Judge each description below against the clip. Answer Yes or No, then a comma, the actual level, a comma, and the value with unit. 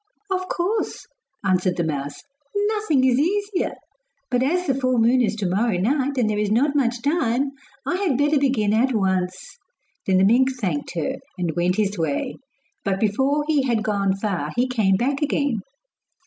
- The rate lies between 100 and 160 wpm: No, average, 175 wpm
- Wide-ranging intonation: Yes, wide, 6.5 semitones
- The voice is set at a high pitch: Yes, high, 240 Hz